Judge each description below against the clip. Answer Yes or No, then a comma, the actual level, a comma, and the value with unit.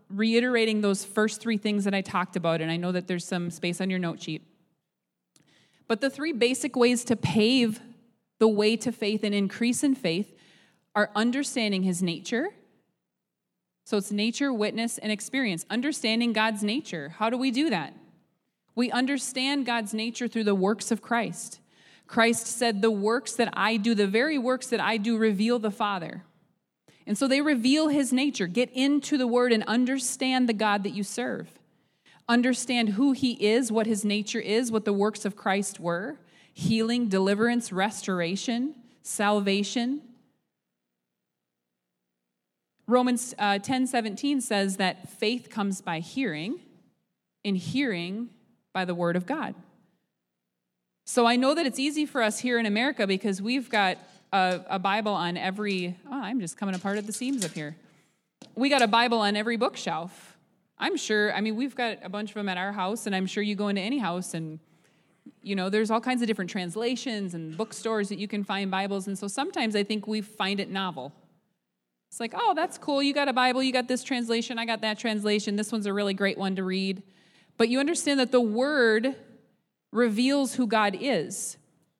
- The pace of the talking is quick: No, average, 180 wpm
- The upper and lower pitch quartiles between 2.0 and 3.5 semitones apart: No, average, 4.1 semitones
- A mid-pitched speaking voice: No, high, 215 Hz